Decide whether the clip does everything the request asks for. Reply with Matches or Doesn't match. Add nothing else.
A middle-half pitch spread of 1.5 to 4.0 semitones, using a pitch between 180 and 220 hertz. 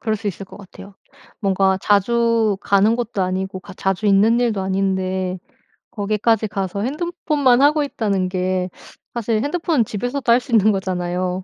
Matches